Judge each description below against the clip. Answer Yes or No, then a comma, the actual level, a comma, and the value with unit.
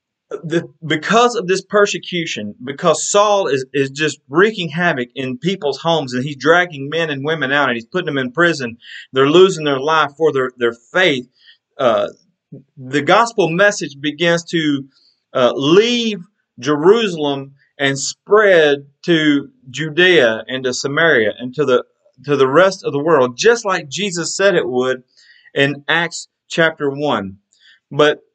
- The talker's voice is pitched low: No, medium, 155 Hz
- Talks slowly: No, average, 150 wpm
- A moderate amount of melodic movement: Yes, average, 4.5 semitones